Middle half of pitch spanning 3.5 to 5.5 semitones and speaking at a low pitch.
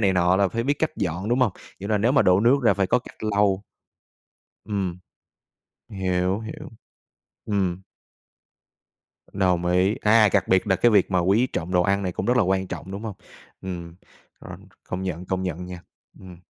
No: average, 2.7 semitones; very low, 95 Hz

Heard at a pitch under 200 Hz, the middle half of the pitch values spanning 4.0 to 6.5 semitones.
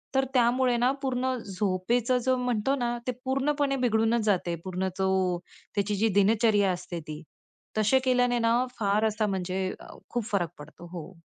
No: high, 220 Hz; average, 4.6 semitones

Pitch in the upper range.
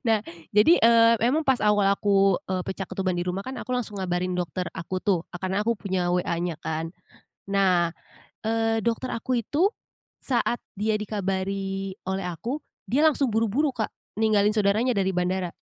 Yes: high, 200 Hz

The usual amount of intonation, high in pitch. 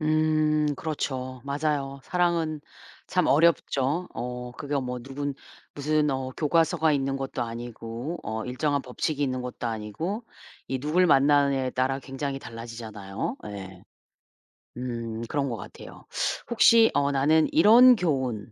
No: average, 3.7 semitones; medium, 140 Hz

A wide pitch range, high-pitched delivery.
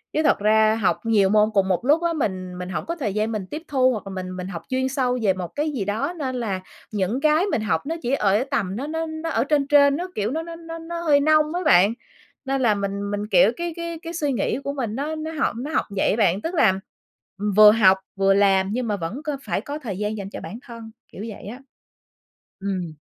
Yes: wide, 7.0 semitones; high, 230 Hz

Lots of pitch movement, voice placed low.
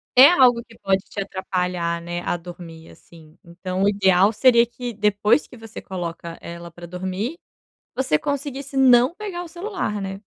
No: wide, 6.2 semitones; high, 200 Hz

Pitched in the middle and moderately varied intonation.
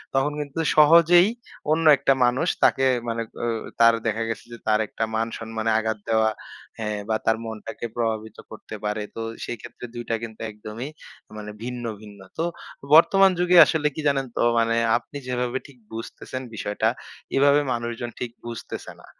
No: low, 115 Hz; average, 3.7 semitones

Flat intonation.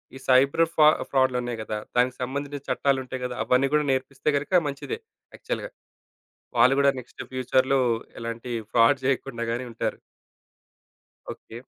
Yes: narrow, 2.0 semitones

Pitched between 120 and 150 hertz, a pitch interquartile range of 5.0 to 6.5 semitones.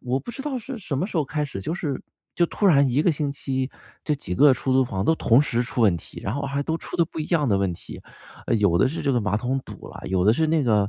Yes: medium, 140 Hz; wide, 5.4 semitones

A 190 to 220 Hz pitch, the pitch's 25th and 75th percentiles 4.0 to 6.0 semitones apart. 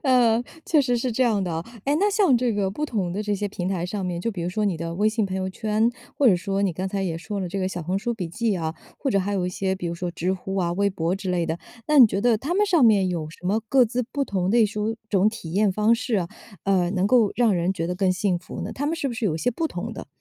Yes: high, 200 Hz; average, 4.3 semitones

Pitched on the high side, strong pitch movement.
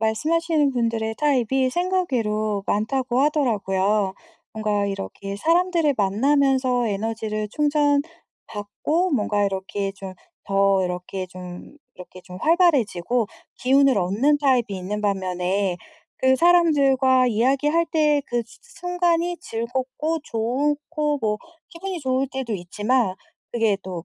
Yes: high, 240 Hz; wide, 6.4 semitones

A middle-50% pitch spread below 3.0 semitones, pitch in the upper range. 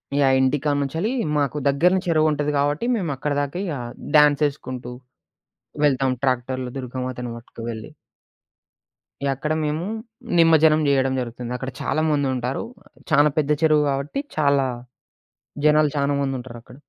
No: narrow, 2.6 semitones; medium, 140 Hz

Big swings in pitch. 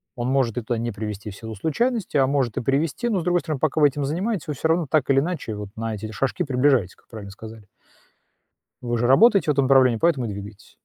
Yes: wide, 5.8 semitones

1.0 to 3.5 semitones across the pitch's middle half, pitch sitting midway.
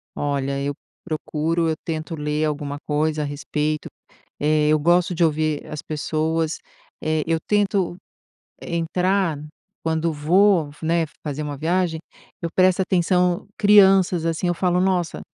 Yes: average, 2.8 semitones; medium, 160 Hz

